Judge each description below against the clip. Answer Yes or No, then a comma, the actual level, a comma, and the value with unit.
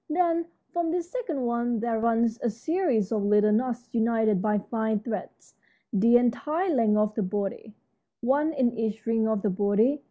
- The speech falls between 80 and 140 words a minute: No, average, 170 wpm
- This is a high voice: Yes, high, 230 Hz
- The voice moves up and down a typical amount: Yes, average, 3.7 semitones